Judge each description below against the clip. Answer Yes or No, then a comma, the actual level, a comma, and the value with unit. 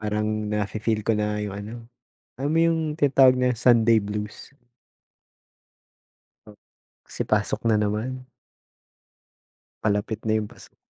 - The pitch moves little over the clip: No, average, 3.3 semitones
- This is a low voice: Yes, low, 110 Hz